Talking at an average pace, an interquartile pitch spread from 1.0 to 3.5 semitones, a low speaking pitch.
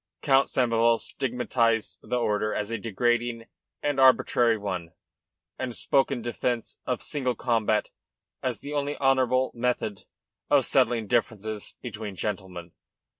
No: slow, 125 wpm; average, 3.0 semitones; low, 120 Hz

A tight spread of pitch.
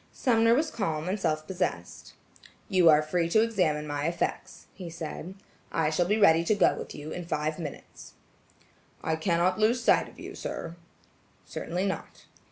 No: average, 4.1 semitones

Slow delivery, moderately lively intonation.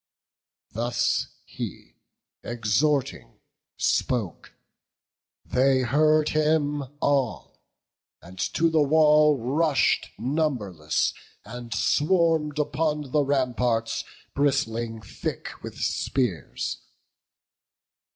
Yes: slow, 75 wpm; average, 4.4 semitones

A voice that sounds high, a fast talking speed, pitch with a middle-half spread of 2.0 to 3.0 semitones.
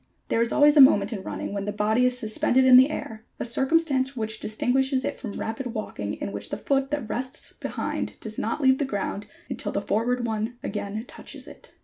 No: high, 235 Hz; fast, 215 wpm; average, 3.7 semitones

